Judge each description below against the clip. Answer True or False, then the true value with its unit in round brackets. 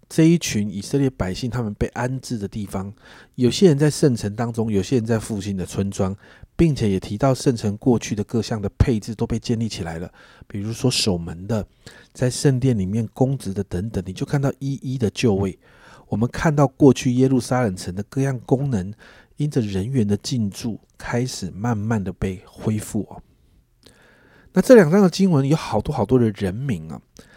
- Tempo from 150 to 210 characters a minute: False (285 characters per minute)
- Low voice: True (115 Hz)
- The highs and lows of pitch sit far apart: False (4.6 semitones)